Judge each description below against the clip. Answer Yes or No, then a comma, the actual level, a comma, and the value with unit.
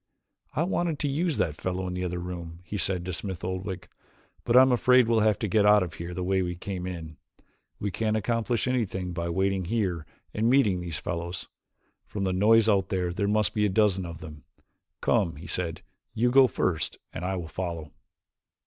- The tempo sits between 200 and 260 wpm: Yes, fast, 205 wpm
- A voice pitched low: Yes, very low, 95 Hz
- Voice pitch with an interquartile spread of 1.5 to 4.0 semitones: Yes, average, 3.7 semitones